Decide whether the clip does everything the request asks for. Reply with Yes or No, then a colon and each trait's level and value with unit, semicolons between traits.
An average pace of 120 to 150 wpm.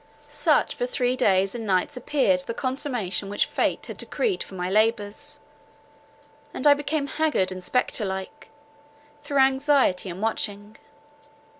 Yes: average, 140 wpm